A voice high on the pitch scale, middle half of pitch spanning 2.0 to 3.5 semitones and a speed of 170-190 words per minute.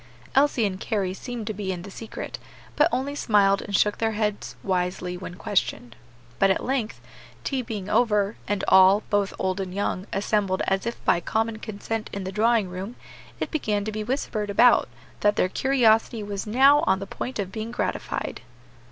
Yes: high, 210 Hz; average, 2.8 semitones; average, 185 wpm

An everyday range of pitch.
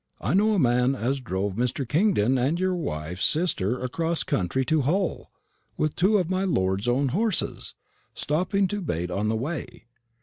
No: wide, 8.0 semitones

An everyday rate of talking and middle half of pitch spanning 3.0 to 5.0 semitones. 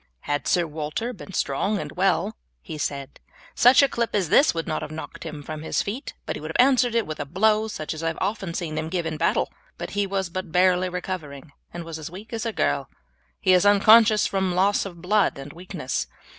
No: fast, 230 wpm; average, 4.7 semitones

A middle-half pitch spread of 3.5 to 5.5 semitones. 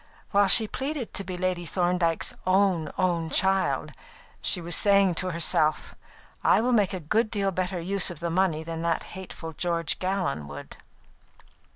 No: average, 2.8 semitones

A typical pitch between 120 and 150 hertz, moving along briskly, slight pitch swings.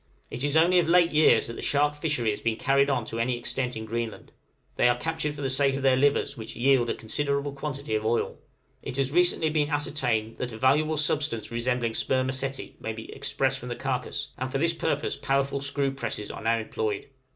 No: low, 135 Hz; fast, 220 wpm; average, 3.6 semitones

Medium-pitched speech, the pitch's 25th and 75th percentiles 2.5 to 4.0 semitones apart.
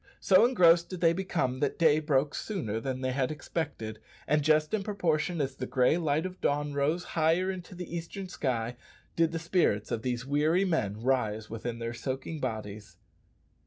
No: medium, 150 Hz; average, 5.1 semitones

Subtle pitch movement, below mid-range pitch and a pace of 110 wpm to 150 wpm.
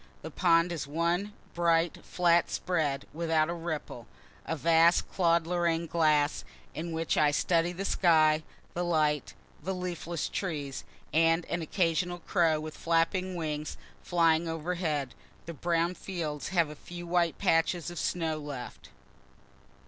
No: narrow, 1.8 semitones; medium, 165 Hz; average, 140 wpm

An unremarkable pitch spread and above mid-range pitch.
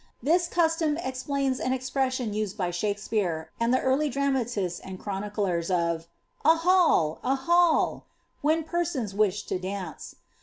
No: wide, 7.4 semitones; very high, 250 Hz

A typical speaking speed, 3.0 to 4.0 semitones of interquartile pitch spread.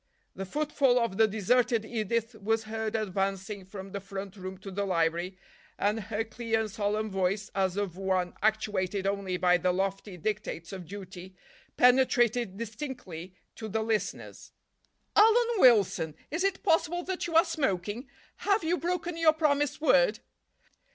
No: average, 150 wpm; average, 4.5 semitones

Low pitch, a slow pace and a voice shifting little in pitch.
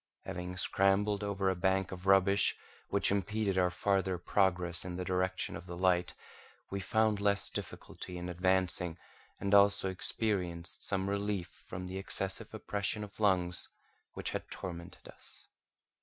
No: very low, 95 Hz; average, 145 wpm; narrow, 1.9 semitones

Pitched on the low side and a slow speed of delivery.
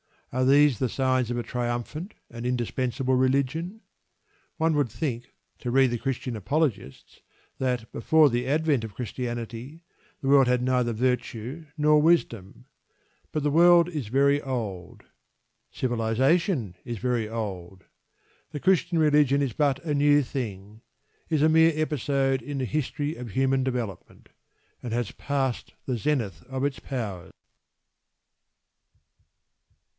Yes: low, 130 Hz; slow, 130 wpm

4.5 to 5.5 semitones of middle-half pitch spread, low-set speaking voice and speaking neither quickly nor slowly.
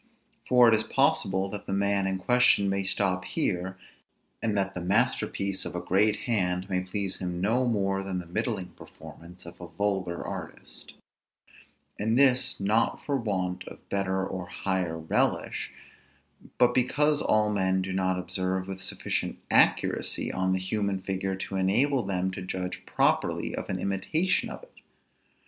No: narrow, 2.4 semitones; very low, 95 Hz; average, 160 wpm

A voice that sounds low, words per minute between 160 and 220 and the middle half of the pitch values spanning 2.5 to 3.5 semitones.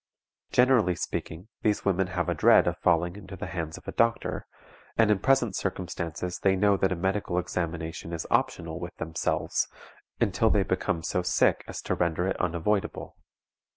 Yes: very low, 90 Hz; average, 170 wpm; average, 3.1 semitones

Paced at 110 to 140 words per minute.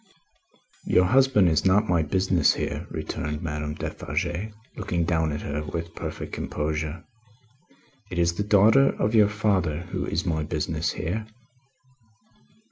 Yes: slow, 135 wpm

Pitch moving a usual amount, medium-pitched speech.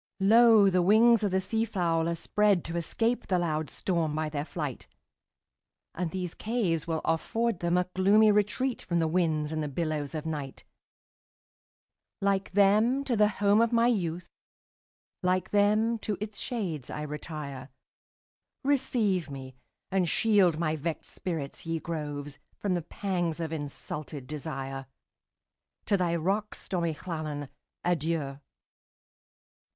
Yes: average, 4.9 semitones; medium, 175 Hz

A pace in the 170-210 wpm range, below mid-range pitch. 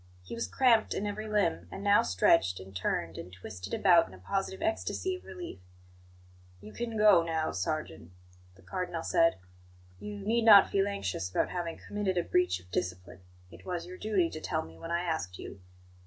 No: average, 190 wpm; medium, 170 Hz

